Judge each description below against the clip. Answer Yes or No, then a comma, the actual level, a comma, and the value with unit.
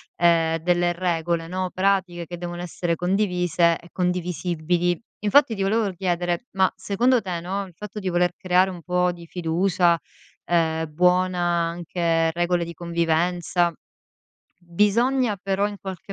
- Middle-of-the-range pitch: Yes, medium, 180 Hz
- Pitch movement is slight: Yes, narrow, 1.8 semitones